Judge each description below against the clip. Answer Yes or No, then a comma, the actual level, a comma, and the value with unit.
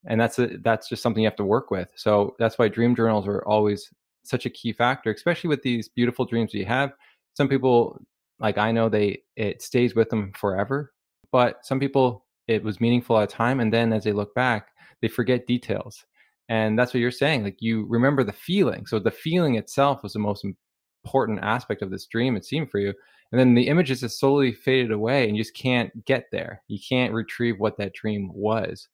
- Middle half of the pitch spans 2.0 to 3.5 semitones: Yes, average, 3.0 semitones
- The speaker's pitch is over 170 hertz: No, low, 115 Hz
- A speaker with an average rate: No, fast, 220 wpm